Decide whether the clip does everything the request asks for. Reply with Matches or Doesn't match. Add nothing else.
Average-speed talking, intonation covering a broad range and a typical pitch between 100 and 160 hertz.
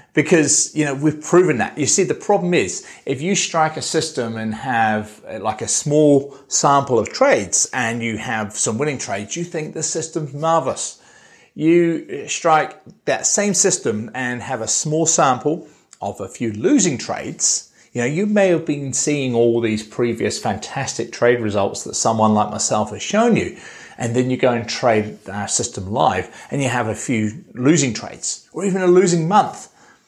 Matches